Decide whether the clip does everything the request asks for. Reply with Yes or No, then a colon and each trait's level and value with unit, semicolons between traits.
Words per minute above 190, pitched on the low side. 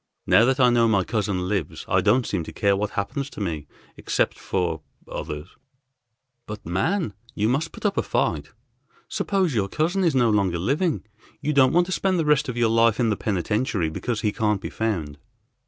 Yes: average, 200 wpm; low, 110 Hz